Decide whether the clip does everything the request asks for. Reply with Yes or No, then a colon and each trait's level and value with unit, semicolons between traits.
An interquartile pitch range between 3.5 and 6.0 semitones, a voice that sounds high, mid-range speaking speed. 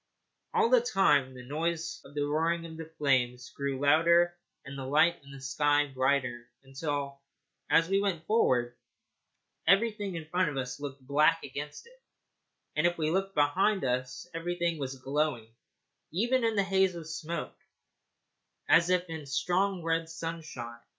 No: average, 3.9 semitones; medium, 155 Hz; average, 155 wpm